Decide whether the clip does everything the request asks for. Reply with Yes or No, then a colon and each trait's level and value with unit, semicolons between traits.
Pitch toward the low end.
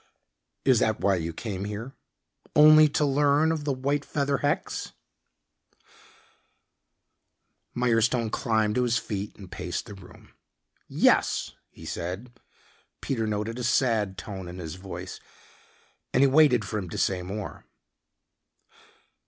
Yes: low, 115 Hz